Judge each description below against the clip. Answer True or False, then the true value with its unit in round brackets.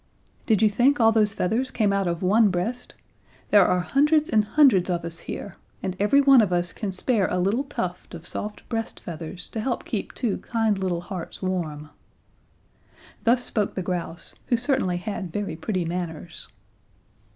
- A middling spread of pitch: True (4.3 semitones)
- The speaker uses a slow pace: False (180 wpm)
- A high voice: True (200 Hz)